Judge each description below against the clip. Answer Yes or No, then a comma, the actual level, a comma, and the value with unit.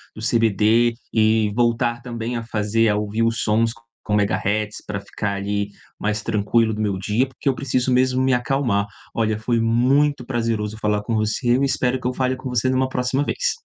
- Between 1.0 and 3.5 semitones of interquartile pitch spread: Yes, average, 2.9 semitones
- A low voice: Yes, low, 115 Hz